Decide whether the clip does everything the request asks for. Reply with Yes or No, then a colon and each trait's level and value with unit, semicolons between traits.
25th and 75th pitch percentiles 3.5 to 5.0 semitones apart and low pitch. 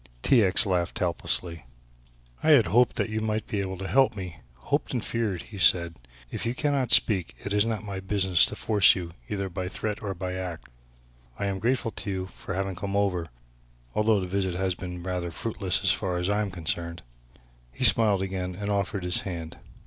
No: narrow, 2.6 semitones; very low, 95 Hz